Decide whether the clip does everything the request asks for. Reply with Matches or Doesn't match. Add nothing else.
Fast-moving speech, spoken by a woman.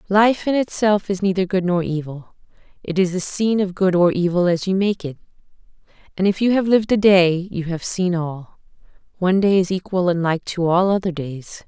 Matches